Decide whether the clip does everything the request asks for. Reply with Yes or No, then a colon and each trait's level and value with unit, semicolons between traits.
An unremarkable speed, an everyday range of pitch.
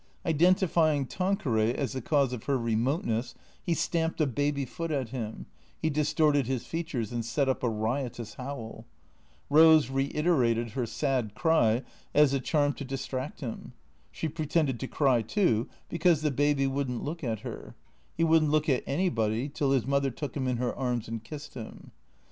Yes: average, 180 wpm; average, 4.2 semitones